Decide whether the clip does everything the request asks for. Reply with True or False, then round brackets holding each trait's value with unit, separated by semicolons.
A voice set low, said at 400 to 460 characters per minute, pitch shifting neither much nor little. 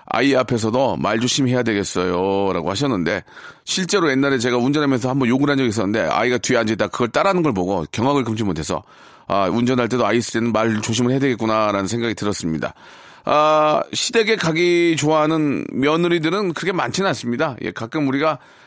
False (125 Hz; 420 characters per minute; 5.7 semitones)